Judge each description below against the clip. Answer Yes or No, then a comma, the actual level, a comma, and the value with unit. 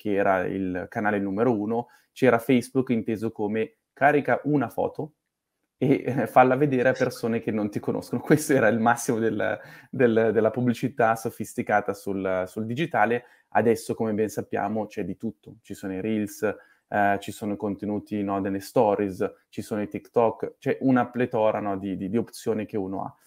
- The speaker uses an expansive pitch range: No, average, 3.0 semitones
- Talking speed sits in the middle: No, fast, 180 wpm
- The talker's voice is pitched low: Yes, low, 110 Hz